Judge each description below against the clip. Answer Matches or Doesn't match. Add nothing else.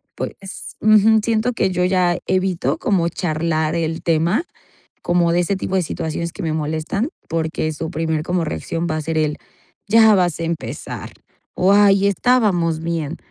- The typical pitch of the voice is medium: Matches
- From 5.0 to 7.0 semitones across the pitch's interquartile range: Doesn't match